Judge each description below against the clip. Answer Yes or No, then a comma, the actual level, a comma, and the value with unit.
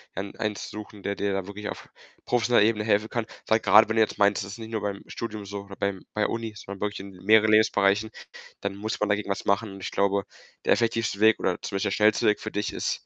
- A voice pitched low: Yes, low, 105 Hz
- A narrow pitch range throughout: Yes, narrow, 1.7 semitones